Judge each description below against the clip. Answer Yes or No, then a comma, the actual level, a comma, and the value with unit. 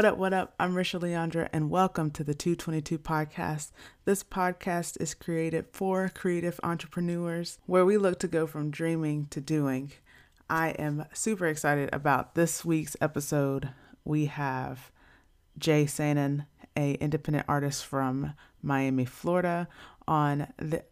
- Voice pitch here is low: No, medium, 155 Hz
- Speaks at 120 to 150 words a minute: Yes, average, 140 wpm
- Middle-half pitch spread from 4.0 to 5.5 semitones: No, average, 2.9 semitones